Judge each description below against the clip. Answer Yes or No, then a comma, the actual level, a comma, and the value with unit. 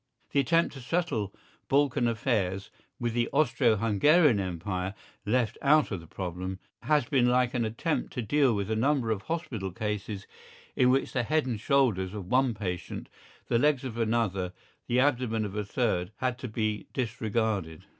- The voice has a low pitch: Yes, low, 115 Hz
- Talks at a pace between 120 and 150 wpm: No, average, 170 wpm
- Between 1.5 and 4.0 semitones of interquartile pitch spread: No, average, 4.5 semitones